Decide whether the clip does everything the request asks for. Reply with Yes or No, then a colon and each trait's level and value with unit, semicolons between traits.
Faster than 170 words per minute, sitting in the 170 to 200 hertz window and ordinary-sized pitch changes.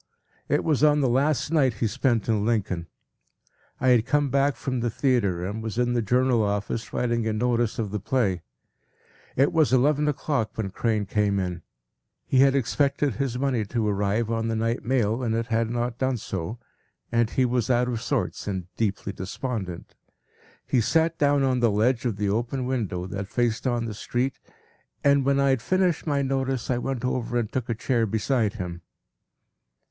No: average, 190 wpm; low, 120 Hz; average, 3.6 semitones